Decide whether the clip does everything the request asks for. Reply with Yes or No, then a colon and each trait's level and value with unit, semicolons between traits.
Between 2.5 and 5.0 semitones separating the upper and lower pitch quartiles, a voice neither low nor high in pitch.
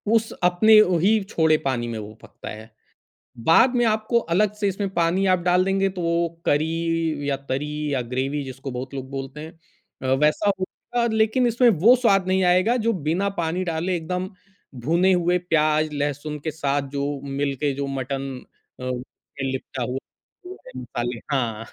No: wide, 5.6 semitones; medium, 160 Hz